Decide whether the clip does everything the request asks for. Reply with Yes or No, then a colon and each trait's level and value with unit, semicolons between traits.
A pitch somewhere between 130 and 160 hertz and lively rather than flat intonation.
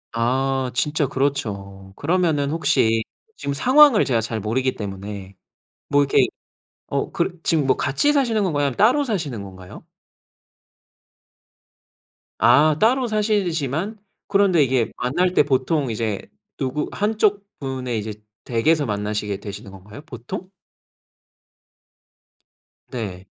Yes: low, 135 Hz; wide, 7.9 semitones